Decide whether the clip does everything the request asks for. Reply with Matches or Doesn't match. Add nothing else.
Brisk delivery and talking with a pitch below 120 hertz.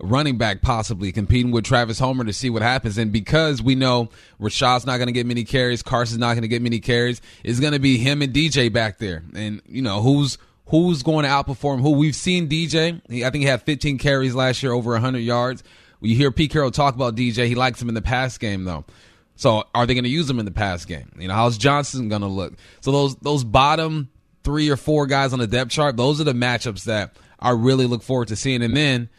Doesn't match